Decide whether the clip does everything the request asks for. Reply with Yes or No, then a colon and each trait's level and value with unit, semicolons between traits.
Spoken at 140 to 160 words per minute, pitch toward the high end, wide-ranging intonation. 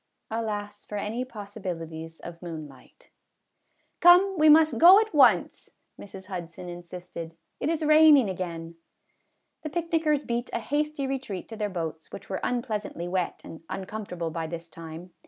Yes: average, 155 wpm; high, 205 Hz; wide, 8.7 semitones